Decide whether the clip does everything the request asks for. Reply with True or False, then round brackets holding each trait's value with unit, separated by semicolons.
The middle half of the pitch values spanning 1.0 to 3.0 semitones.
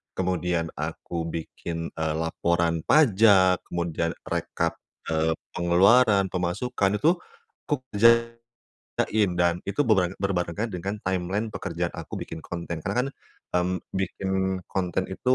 True (2.4 semitones)